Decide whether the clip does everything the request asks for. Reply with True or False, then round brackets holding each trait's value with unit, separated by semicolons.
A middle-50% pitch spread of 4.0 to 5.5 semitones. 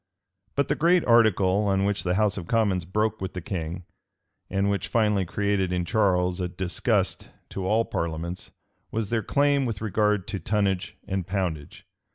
False (3.0 semitones)